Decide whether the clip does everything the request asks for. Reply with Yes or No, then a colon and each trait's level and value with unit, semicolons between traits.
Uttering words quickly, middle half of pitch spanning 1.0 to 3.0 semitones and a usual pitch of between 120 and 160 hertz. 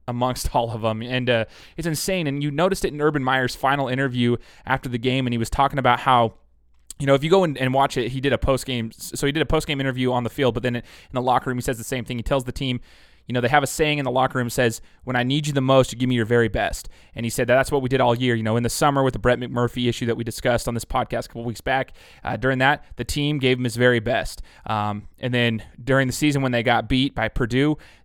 Yes: fast, 295 wpm; narrow, 2.4 semitones; low, 125 Hz